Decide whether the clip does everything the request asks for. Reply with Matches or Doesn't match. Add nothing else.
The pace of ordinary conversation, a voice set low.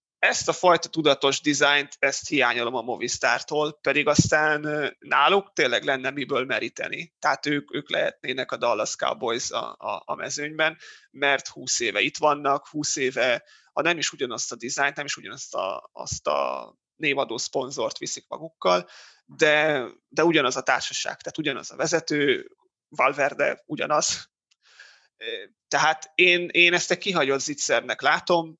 Doesn't match